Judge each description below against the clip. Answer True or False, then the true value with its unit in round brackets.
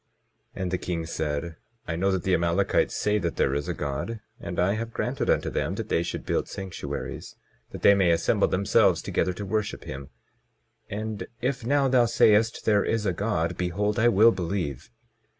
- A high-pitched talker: False (95 Hz)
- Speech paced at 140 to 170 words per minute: False (185 wpm)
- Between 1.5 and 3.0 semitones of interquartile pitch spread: False (4.3 semitones)